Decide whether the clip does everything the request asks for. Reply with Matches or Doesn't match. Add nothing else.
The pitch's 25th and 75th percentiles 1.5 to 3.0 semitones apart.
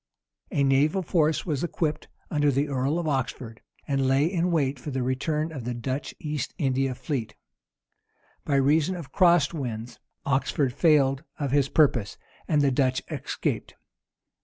Matches